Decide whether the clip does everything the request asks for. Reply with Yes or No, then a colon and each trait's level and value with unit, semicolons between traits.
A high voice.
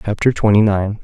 No: low, 105 Hz